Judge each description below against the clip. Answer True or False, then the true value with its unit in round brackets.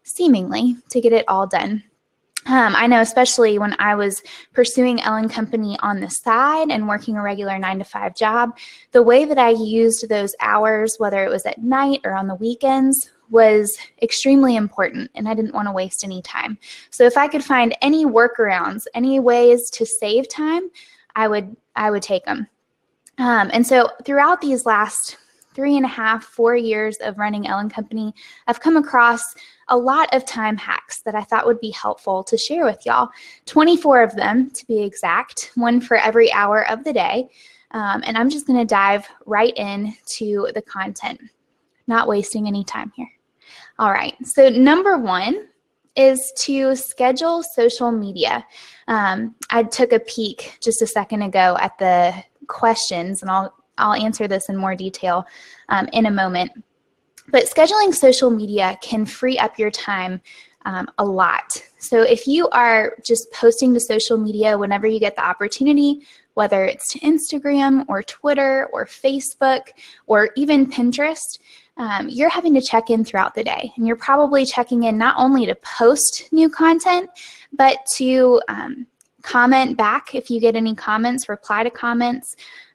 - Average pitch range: True (3.9 semitones)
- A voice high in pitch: True (235 Hz)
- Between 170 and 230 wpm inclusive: True (175 wpm)